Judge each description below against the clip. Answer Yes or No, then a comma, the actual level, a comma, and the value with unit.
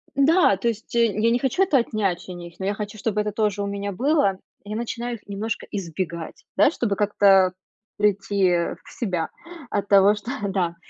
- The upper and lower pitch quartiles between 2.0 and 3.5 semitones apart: Yes, average, 3.1 semitones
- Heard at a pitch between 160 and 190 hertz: No, high, 205 Hz